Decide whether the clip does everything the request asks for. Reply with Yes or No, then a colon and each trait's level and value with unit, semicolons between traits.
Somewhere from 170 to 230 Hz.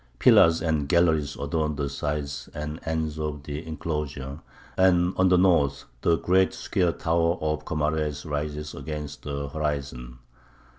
No: very low, 75 Hz